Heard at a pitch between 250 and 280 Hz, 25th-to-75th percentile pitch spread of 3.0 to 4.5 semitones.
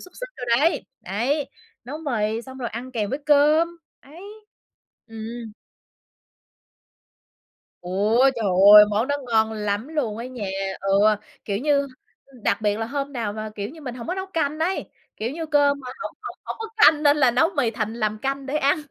No: very high, 255 Hz; average, 5.0 semitones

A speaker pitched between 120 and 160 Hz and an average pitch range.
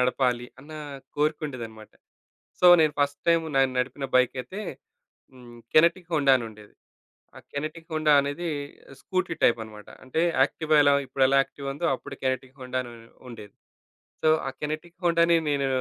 Yes: medium, 140 Hz; average, 3.7 semitones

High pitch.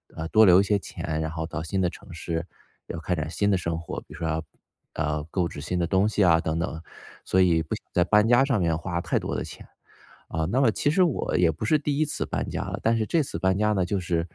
No: very low, 90 Hz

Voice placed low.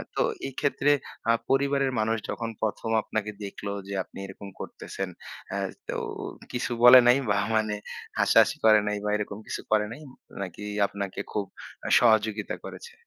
Yes: low, 110 Hz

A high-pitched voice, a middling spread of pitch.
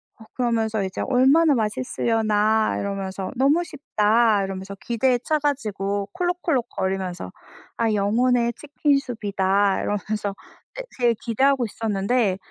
Yes: high, 220 Hz; average, 4.3 semitones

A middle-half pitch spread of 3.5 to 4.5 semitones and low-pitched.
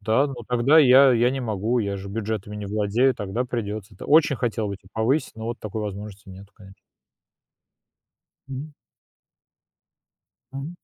Yes: average, 4.0 semitones; low, 110 Hz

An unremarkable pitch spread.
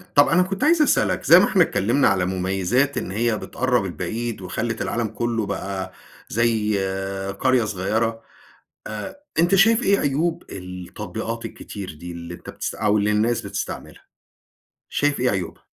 No: wide, 5.7 semitones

